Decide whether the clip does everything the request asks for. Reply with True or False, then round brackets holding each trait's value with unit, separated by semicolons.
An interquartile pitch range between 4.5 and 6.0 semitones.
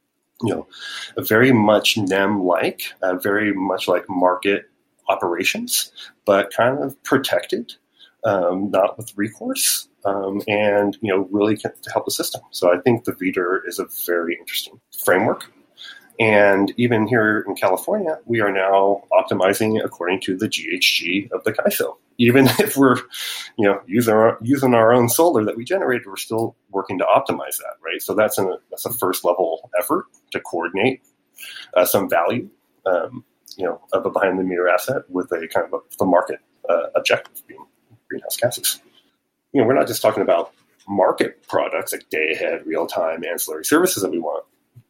False (4.1 semitones)